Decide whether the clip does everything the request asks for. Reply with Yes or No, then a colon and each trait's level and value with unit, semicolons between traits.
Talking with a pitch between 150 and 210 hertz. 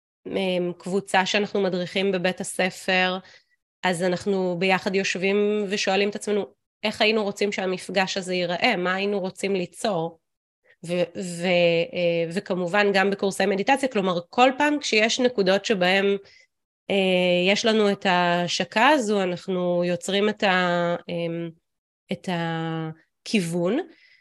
Yes: high, 190 Hz